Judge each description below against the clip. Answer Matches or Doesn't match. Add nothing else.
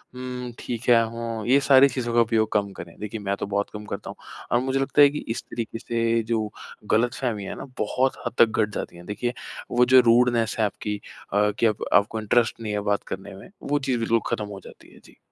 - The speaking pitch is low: Matches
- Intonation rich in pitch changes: Doesn't match